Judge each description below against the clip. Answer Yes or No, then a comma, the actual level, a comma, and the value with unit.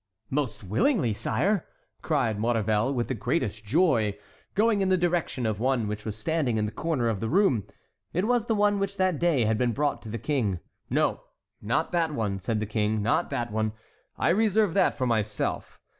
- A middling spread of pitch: No, wide, 8.0 semitones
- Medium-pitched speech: No, low, 125 Hz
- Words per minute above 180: Yes, average, 195 wpm